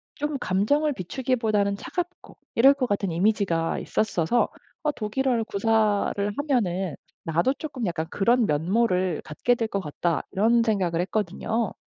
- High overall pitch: Yes, high, 215 Hz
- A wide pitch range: No, average, 5.0 semitones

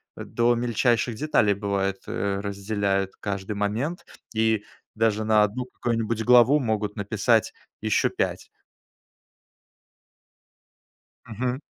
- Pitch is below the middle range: Yes, low, 110 Hz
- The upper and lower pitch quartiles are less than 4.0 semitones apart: Yes, average, 2.8 semitones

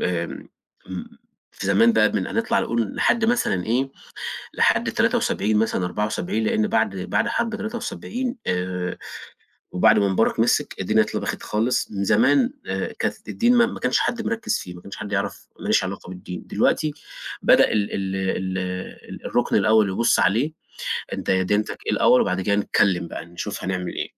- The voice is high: No, low, 105 Hz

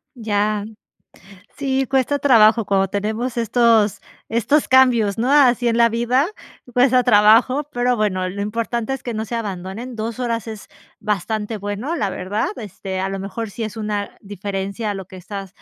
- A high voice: Yes, high, 220 Hz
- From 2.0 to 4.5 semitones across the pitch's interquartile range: Yes, average, 3.1 semitones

